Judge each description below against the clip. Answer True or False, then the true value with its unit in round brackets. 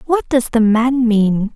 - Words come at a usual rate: True (190 wpm)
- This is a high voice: True (230 Hz)